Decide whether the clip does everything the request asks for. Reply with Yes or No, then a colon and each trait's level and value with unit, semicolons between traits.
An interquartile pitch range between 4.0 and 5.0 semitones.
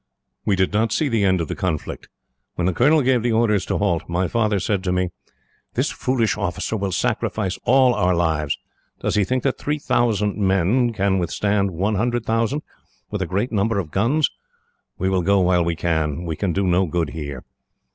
Yes: average, 4.3 semitones